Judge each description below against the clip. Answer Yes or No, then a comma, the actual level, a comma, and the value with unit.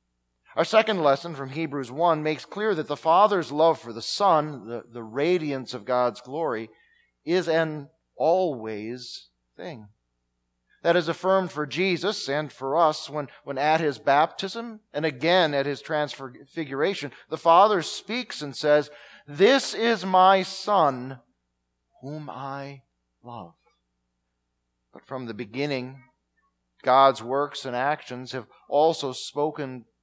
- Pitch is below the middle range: No, medium, 145 Hz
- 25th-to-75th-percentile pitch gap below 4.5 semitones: No, average, 4.9 semitones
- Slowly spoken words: Yes, slow, 130 wpm